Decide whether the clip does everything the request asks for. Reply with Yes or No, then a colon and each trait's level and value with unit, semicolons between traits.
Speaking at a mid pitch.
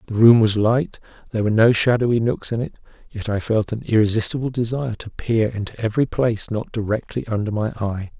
No: low, 110 Hz